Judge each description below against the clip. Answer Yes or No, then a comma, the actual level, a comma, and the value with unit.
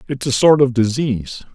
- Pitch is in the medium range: No, low, 130 Hz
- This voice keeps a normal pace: Yes, average, 195 wpm